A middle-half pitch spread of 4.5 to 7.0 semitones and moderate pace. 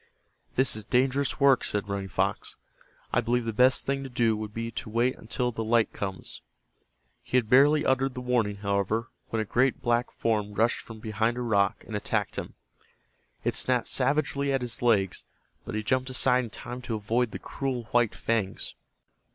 No: average, 2.8 semitones; average, 185 wpm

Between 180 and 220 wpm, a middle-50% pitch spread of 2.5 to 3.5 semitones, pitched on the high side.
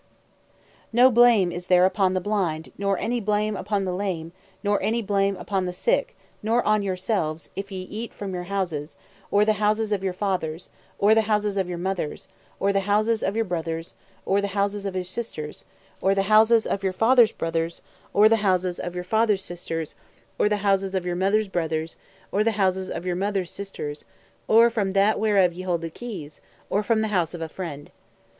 Yes: fast, 205 wpm; average, 2.9 semitones; high, 195 Hz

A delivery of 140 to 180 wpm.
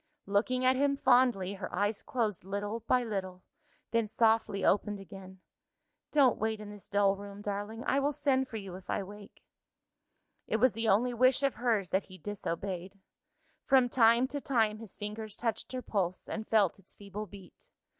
Yes: average, 175 wpm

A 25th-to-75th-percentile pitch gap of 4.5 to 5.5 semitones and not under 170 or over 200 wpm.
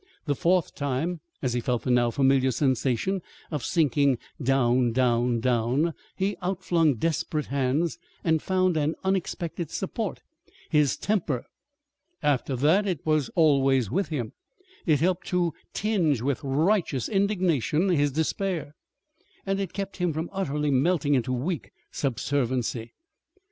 No: average, 5.2 semitones; slow, 135 wpm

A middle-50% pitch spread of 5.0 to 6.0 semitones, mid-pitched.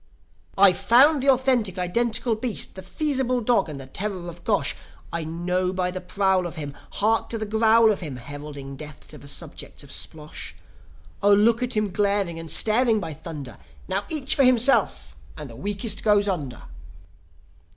No: wide, 5.5 semitones; high, 200 Hz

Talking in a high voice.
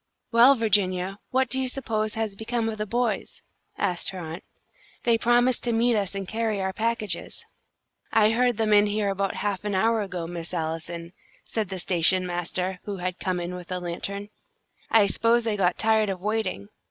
Yes: high, 205 Hz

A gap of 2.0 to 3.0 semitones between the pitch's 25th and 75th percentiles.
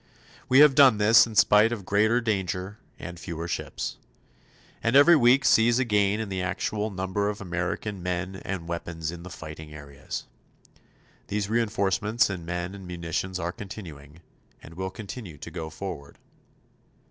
No: average, 4.0 semitones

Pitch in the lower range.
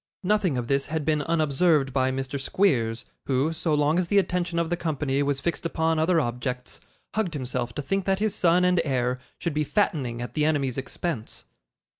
No: medium, 150 Hz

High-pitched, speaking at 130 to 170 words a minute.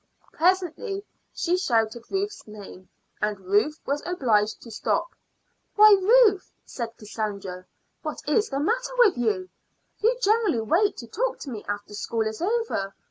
Yes: very high, 280 Hz; average, 145 wpm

